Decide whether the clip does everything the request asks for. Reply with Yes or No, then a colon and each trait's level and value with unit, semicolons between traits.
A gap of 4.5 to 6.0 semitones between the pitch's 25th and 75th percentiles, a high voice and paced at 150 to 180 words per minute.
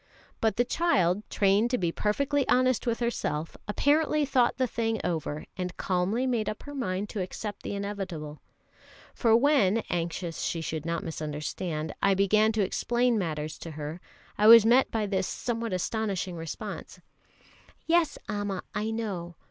Yes: average, 5.2 semitones; high, 205 Hz; average, 155 wpm